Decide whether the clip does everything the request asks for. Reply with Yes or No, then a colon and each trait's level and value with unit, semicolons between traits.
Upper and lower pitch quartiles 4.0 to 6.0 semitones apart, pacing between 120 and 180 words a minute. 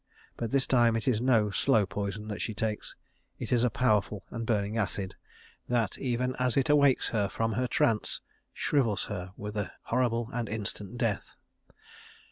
No: average, 2.9 semitones; average, 170 wpm